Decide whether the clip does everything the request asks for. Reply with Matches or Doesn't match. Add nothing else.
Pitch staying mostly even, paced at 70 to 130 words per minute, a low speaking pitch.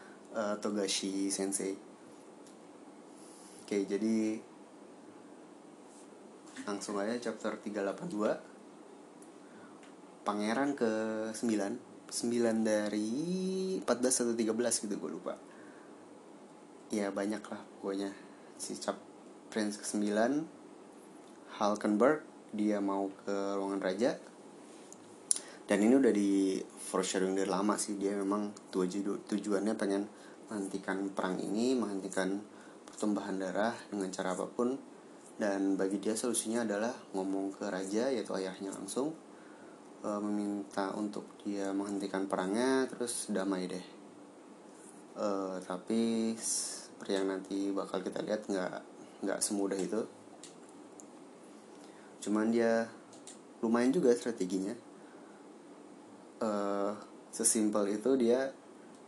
Matches